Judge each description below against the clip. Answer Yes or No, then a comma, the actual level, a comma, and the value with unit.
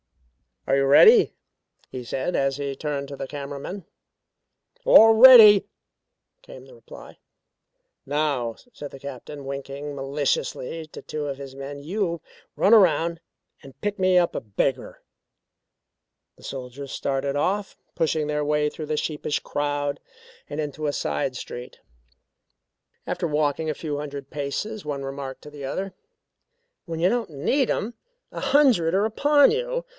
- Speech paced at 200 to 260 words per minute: No, average, 150 wpm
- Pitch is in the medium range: Yes, medium, 150 Hz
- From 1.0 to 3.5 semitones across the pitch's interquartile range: No, average, 5.1 semitones